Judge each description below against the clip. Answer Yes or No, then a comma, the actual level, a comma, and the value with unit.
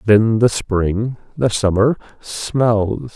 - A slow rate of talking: Yes, slow, 115 wpm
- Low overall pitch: Yes, low, 110 Hz